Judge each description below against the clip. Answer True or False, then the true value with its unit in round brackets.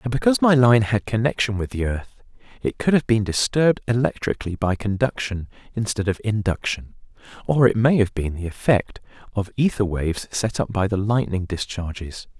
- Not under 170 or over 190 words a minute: True (175 wpm)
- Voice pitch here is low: True (110 Hz)